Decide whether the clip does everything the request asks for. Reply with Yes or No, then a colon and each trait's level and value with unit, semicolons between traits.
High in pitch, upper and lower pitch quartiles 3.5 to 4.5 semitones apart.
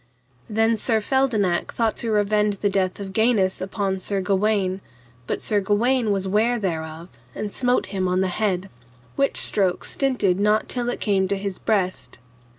No: high, 205 Hz; narrow, 2.6 semitones